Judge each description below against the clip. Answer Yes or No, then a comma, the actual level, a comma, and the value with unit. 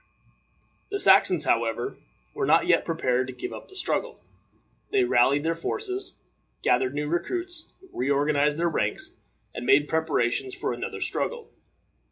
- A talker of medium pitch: Yes, medium, 150 Hz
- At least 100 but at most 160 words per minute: Yes, average, 140 wpm